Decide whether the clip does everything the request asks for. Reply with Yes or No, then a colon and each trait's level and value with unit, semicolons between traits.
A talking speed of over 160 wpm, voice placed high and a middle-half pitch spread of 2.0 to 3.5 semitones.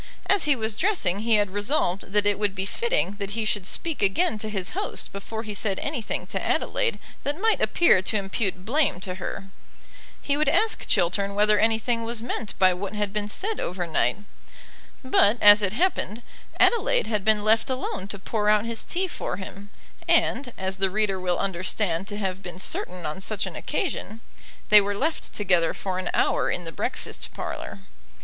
Yes: average, 190 wpm; high, 205 Hz; average, 3.2 semitones